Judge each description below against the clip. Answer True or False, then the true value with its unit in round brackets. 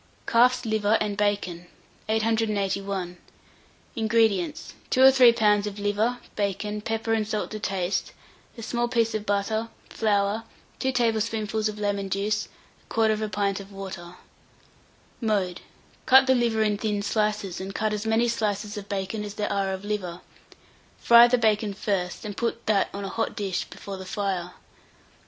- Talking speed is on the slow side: False (155 wpm)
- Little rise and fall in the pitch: True (2.0 semitones)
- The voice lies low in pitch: False (210 Hz)